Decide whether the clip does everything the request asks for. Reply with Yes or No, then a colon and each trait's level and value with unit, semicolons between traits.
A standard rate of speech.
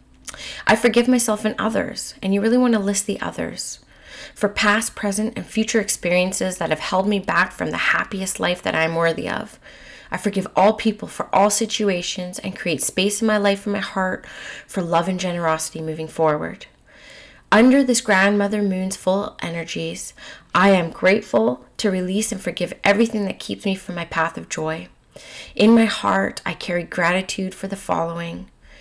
Yes: average, 180 wpm